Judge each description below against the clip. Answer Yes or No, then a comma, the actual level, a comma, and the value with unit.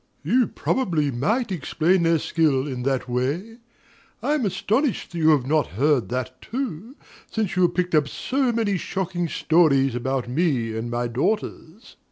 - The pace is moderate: Yes, average, 175 wpm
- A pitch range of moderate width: No, wide, 7.2 semitones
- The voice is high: No, medium, 160 Hz